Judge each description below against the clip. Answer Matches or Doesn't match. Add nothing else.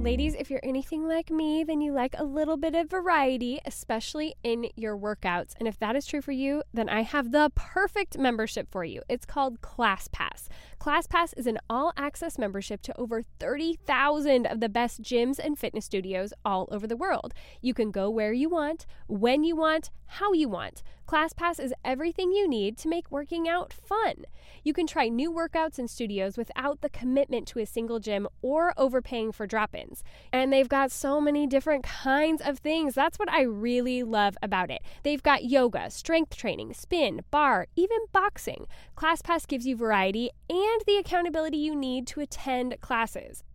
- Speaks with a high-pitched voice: Matches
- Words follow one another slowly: Doesn't match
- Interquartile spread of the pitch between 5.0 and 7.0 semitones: Matches